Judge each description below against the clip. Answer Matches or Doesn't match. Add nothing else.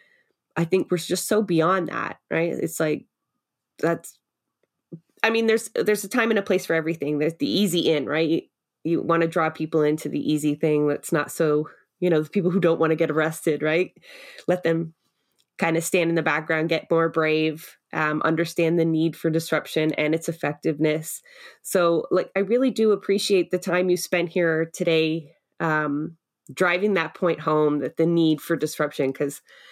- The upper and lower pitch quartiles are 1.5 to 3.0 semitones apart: Matches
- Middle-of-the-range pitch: Matches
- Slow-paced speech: Doesn't match